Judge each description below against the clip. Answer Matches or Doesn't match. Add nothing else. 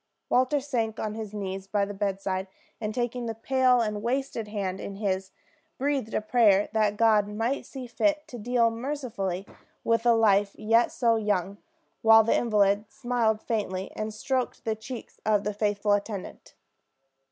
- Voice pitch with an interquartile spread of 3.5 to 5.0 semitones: Doesn't match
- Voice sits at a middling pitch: Doesn't match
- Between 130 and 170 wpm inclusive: Matches